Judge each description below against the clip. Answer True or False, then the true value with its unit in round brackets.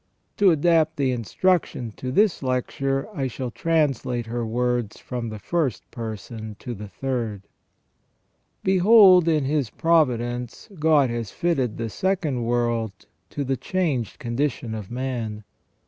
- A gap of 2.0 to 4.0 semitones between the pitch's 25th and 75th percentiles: False (5.1 semitones)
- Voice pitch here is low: True (125 Hz)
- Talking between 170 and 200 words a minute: False (140 wpm)